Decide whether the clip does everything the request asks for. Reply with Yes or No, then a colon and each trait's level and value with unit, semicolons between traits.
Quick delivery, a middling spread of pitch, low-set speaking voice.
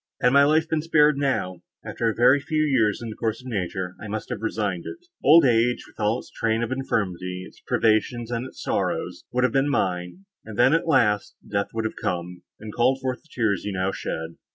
Yes: fast, 225 wpm; average, 4.9 semitones; low, 115 Hz